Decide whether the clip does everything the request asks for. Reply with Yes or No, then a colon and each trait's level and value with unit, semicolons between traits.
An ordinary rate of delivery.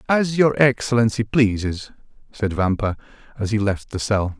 Yes: average, 150 wpm